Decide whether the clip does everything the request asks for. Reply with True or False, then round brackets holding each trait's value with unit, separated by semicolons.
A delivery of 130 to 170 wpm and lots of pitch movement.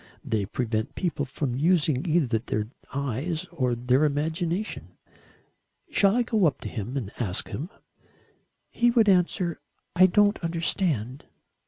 True (135 wpm; 6.2 semitones)